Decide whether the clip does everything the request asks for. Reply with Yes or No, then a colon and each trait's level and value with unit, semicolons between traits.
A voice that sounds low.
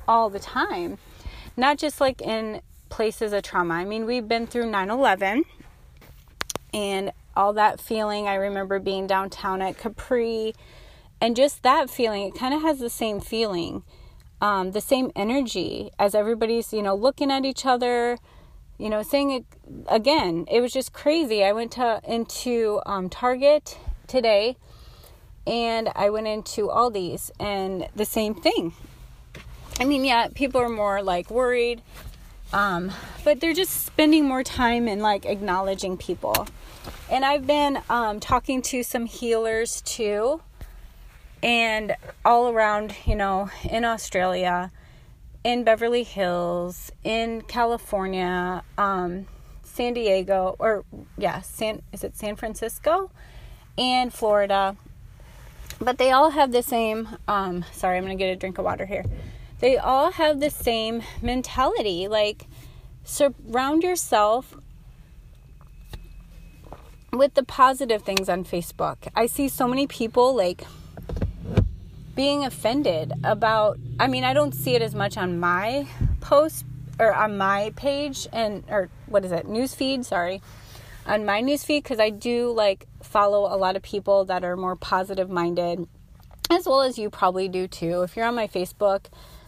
No: high, 220 Hz